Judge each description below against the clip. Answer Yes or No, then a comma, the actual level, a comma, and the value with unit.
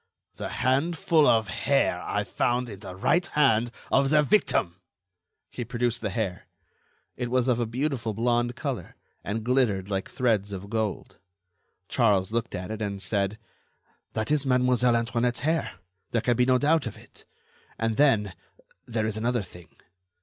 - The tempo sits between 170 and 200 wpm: No, average, 160 wpm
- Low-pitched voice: Yes, low, 115 Hz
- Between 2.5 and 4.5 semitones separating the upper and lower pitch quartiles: Yes, average, 3.3 semitones